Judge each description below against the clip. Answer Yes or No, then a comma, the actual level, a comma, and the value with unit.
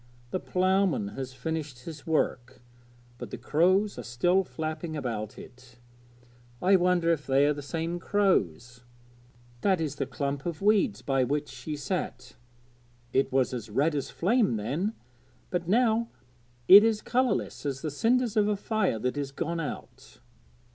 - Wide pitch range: Yes, wide, 6.2 semitones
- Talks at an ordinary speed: Yes, average, 155 wpm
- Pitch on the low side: No, medium, 160 Hz